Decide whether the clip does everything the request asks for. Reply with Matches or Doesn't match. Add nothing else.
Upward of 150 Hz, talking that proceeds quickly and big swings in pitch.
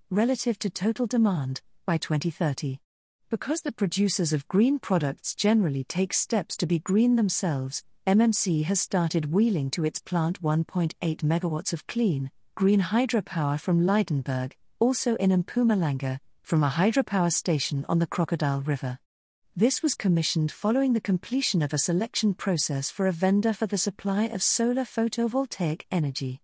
Doesn't match